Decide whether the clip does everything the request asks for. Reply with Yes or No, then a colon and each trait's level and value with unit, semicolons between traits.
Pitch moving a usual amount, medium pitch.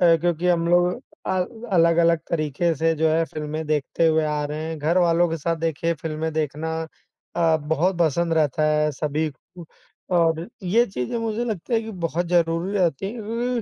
No: narrow, 2.2 semitones; medium, 165 Hz